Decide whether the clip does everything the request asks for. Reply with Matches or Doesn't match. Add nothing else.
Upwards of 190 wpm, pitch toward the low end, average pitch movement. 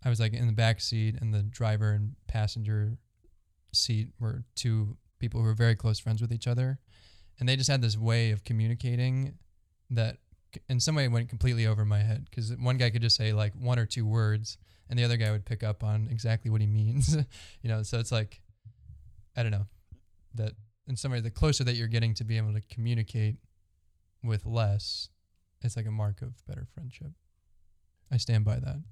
Doesn't match